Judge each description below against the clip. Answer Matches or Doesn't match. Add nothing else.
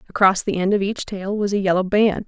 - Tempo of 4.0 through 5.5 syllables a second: Doesn't match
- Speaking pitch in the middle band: Doesn't match